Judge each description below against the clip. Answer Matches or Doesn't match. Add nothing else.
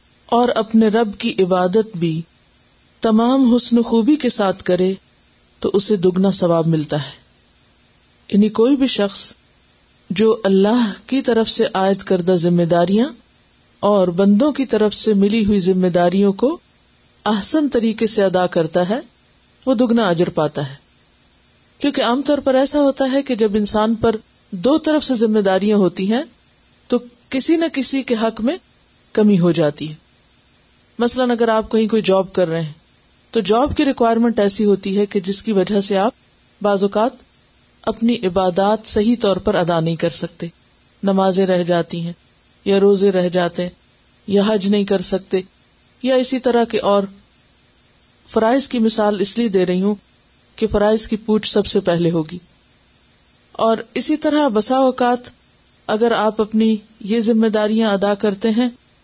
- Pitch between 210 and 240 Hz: Matches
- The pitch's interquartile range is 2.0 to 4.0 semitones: Matches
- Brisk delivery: Doesn't match